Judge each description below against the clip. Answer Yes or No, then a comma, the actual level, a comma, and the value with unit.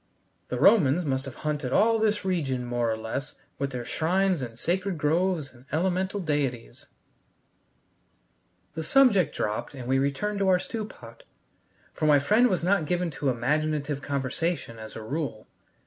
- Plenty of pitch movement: Yes, wide, 5.9 semitones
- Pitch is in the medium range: Yes, medium, 150 Hz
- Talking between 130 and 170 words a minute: Yes, average, 160 wpm